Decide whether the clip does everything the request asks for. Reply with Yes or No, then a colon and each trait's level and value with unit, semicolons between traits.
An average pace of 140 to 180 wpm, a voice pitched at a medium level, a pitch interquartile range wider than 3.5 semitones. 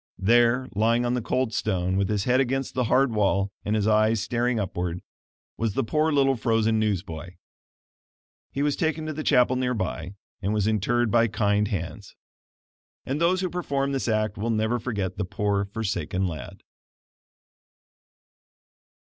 No: average, 160 wpm; low, 110 Hz; average, 4.0 semitones